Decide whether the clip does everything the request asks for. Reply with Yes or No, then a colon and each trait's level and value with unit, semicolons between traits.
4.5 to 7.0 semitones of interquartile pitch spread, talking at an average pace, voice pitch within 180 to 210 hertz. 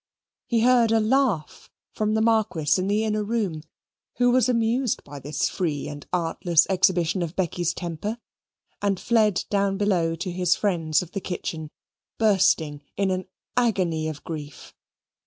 Yes: average, 4.9 semitones; average, 155 wpm; high, 190 Hz